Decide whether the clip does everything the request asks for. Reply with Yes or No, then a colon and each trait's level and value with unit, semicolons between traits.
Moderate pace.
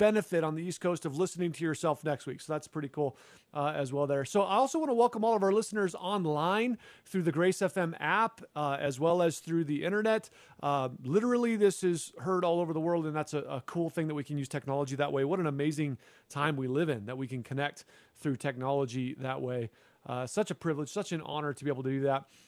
No: fast, 245 wpm